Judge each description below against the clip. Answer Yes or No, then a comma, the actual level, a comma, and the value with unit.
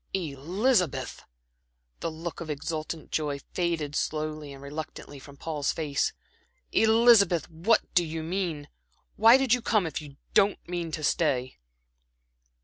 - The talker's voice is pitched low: No, medium, 160 Hz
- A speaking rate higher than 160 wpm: No, slow, 135 wpm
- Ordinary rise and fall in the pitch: Yes, average, 3.9 semitones